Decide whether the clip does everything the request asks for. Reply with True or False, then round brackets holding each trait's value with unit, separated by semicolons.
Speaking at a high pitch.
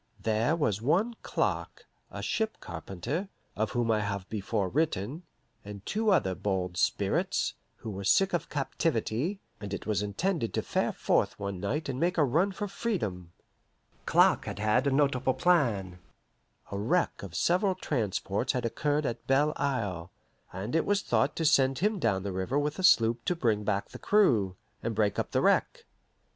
False (120 Hz)